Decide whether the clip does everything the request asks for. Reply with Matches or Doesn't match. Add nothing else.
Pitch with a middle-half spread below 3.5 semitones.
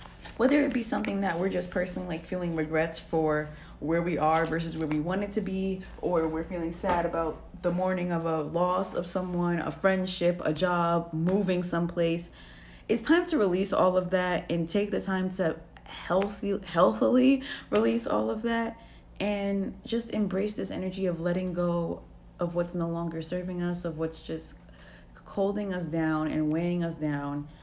Matches